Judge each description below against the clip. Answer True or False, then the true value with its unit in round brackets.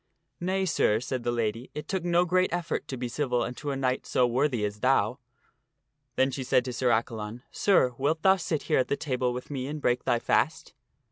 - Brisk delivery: True (230 wpm)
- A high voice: False (130 Hz)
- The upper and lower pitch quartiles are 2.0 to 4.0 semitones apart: False (4.5 semitones)